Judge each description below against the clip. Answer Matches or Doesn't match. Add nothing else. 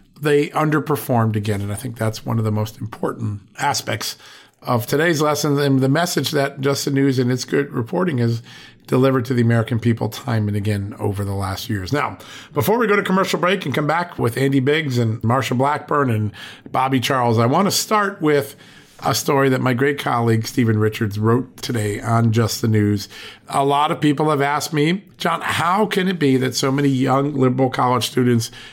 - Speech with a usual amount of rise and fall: Matches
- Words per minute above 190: Matches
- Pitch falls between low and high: Doesn't match